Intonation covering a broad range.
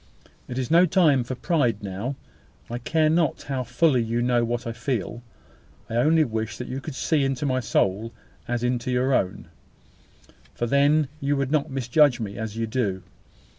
No: average, 3.4 semitones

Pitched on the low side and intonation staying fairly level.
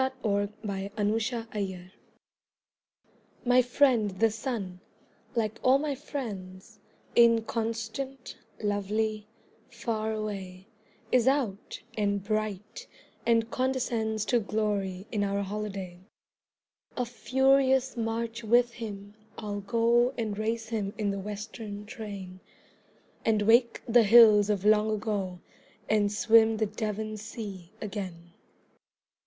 No: high, 215 Hz; narrow, 2.3 semitones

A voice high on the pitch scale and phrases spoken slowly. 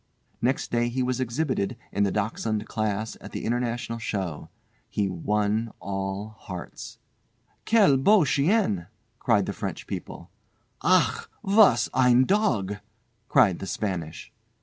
No: low, 110 Hz; slow, 125 wpm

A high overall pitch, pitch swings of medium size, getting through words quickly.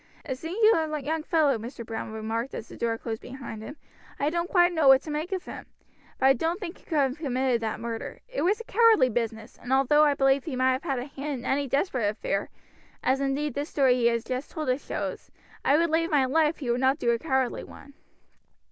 Yes: very high, 270 Hz; average, 4.2 semitones; fast, 230 wpm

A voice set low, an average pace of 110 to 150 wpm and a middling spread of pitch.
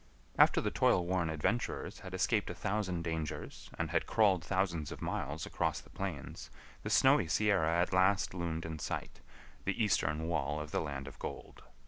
No: very low, 85 Hz; average, 175 wpm; average, 3.9 semitones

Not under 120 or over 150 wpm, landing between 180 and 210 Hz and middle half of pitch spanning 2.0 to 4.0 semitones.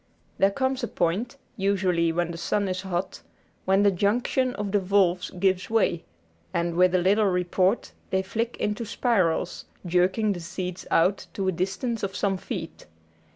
No: average, 165 wpm; high, 190 Hz; narrow, 2.5 semitones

